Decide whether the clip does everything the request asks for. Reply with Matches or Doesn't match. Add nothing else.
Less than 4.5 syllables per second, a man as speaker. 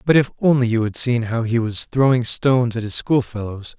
Doesn't match